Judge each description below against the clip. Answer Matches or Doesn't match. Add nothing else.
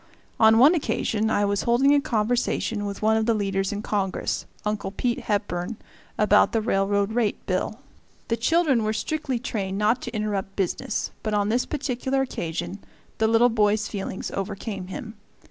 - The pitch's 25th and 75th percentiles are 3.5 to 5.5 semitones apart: Doesn't match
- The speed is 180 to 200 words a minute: Doesn't match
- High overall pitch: Matches